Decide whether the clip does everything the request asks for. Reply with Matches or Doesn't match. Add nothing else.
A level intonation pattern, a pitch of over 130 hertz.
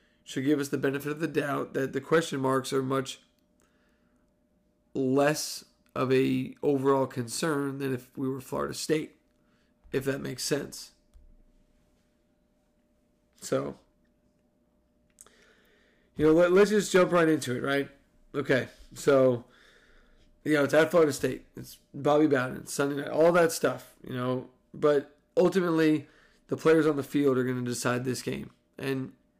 Doesn't match